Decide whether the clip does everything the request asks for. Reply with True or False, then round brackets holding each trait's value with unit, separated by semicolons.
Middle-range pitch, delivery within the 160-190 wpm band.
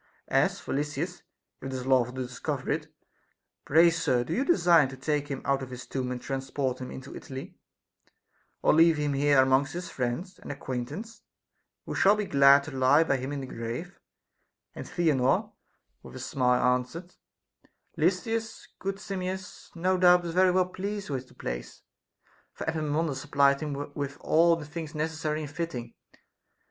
True (145 Hz; 170 wpm)